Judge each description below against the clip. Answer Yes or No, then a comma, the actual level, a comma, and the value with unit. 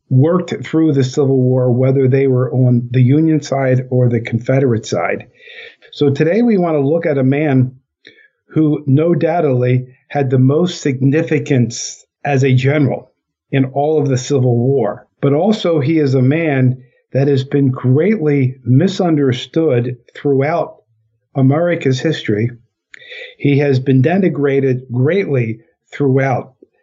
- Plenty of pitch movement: No, average, 3.4 semitones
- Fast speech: No, slow, 135 wpm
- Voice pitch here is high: No, low, 135 Hz